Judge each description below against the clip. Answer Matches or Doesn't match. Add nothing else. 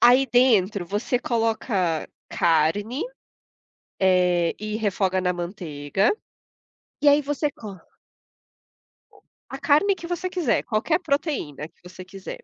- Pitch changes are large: Matches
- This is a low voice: Doesn't match